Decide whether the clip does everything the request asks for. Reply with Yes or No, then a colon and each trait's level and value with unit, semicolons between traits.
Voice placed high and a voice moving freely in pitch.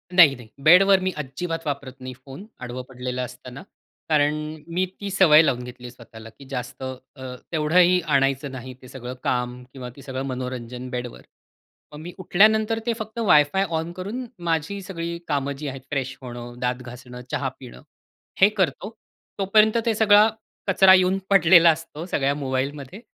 No: medium, 145 Hz; wide, 6.2 semitones